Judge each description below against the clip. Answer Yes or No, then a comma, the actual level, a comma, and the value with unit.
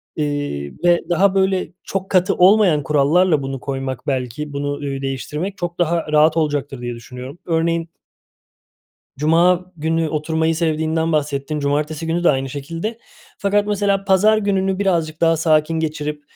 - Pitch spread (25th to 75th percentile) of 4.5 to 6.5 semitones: No, average, 3.7 semitones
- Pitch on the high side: No, medium, 160 Hz